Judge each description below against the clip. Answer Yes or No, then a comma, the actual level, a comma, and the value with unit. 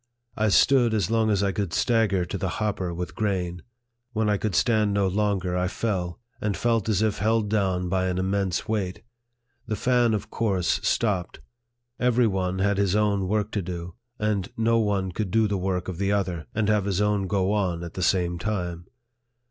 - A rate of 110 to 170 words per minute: No, average, 195 wpm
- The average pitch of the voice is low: Yes, low, 100 Hz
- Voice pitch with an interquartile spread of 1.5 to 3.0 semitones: Yes, average, 2.7 semitones